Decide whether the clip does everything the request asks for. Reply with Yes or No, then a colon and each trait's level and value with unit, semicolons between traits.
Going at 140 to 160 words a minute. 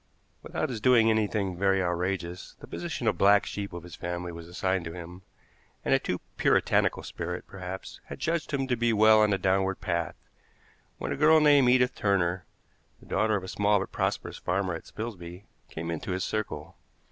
No: average, 190 wpm